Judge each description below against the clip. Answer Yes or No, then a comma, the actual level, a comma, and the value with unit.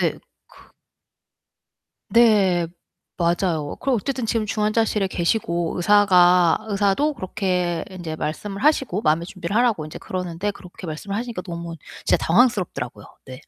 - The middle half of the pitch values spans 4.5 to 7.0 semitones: No, average, 4.0 semitones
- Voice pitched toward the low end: No, medium, 185 Hz